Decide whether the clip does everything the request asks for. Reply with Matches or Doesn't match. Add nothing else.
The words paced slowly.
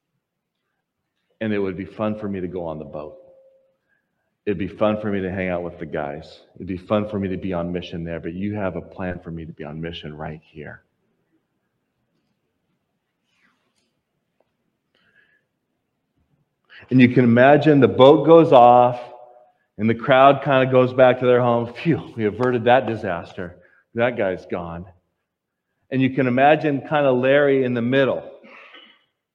Doesn't match